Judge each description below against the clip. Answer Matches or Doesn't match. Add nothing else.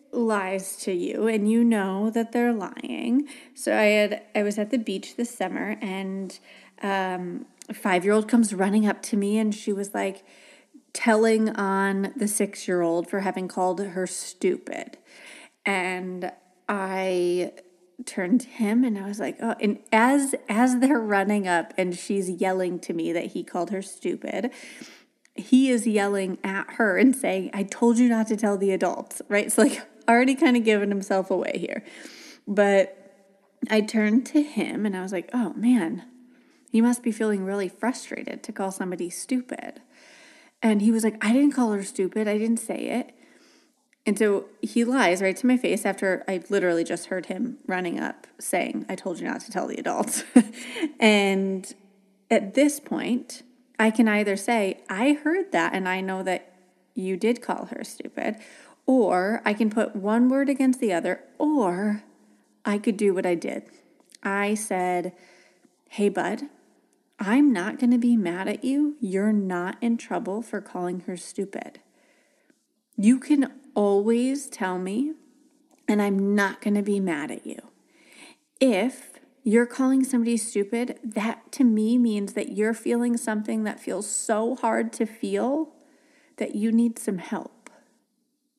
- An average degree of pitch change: Matches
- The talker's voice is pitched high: Matches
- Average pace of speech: Matches